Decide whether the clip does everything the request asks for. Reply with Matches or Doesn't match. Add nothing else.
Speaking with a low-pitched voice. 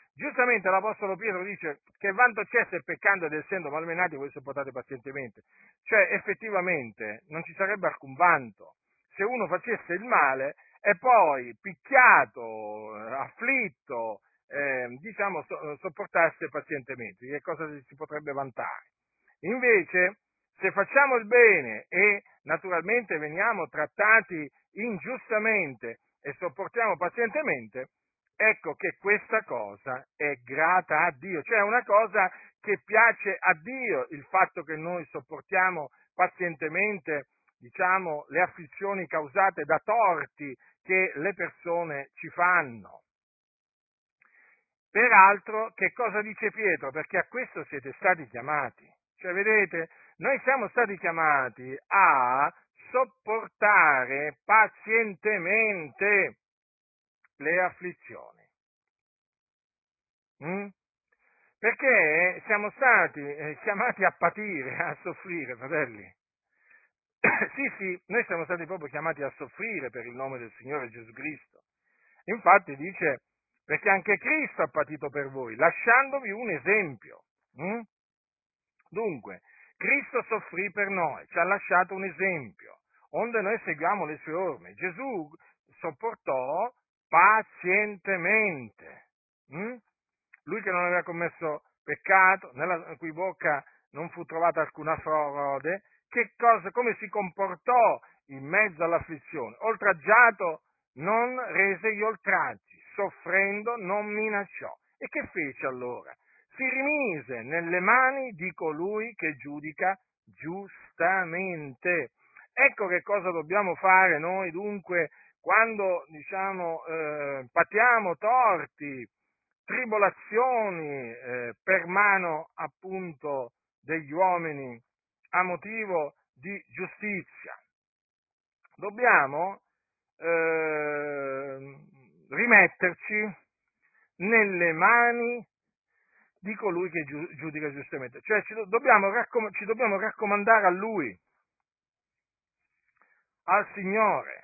Doesn't match